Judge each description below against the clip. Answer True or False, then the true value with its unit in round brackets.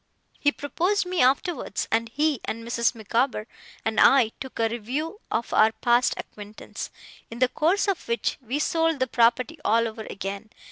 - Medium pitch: False (245 Hz)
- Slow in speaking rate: False (170 wpm)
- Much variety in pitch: False (4.9 semitones)